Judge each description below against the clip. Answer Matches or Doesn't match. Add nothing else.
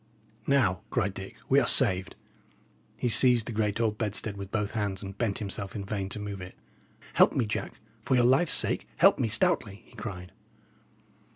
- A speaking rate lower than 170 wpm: Doesn't match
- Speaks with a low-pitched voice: Matches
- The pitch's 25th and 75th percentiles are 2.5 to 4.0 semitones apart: Matches